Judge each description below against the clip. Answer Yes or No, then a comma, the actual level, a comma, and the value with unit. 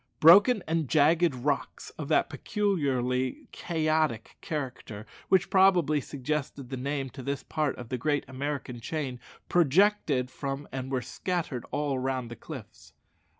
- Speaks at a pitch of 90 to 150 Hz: Yes, medium, 140 Hz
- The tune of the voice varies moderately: Yes, average, 3.7 semitones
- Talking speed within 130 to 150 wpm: Yes, average, 140 wpm